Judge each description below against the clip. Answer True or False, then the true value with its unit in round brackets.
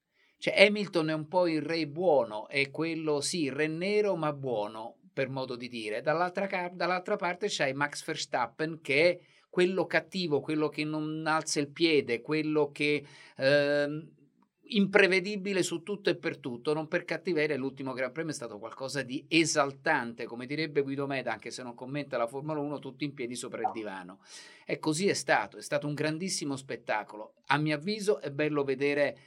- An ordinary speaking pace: False (180 wpm)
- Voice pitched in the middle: True (150 Hz)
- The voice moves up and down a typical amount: True (3.6 semitones)